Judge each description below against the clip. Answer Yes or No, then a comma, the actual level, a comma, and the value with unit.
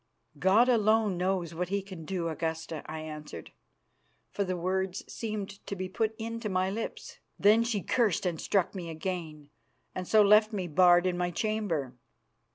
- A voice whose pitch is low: No, medium, 185 Hz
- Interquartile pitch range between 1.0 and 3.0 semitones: No, average, 3.8 semitones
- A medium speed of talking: Yes, average, 165 wpm